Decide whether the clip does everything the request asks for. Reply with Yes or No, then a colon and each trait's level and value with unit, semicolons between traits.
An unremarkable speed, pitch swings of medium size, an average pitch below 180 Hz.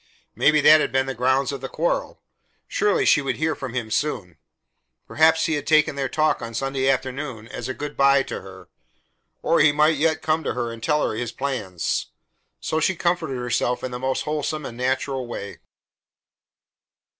Yes: average, 190 wpm; average, 3.7 semitones; low, 135 Hz